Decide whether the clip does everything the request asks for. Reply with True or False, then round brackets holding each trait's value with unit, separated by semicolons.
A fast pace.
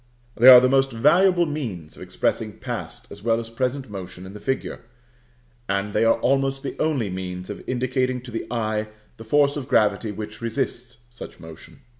False (185 wpm)